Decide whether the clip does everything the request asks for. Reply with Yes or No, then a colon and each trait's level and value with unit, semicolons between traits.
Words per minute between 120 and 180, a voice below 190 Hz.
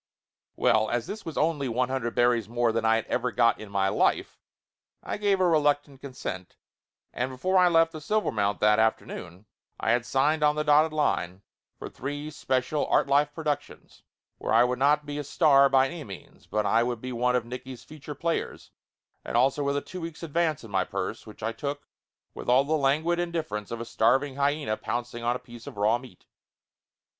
No: average, 200 wpm; low, 135 Hz